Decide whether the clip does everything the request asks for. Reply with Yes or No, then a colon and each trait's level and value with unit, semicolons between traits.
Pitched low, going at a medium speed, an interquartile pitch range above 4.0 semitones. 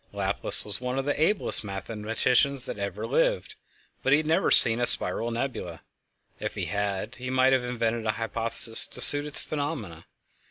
Yes: low, 120 Hz; average, 175 wpm; average, 4.4 semitones